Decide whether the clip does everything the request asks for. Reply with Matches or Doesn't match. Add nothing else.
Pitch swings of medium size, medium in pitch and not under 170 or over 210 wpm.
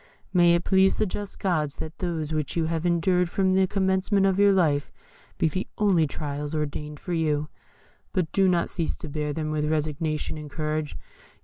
Matches